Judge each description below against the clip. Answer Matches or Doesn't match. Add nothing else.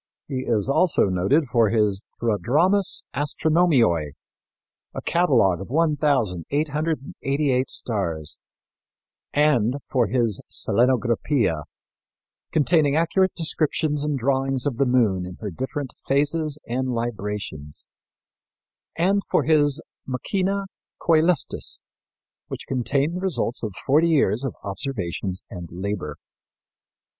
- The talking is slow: Matches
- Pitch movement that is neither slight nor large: Doesn't match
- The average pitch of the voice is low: Matches